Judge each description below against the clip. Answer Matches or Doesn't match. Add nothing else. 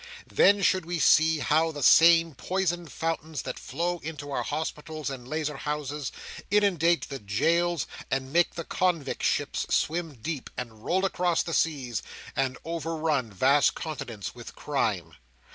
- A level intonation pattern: Doesn't match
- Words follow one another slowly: Doesn't match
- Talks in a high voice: Doesn't match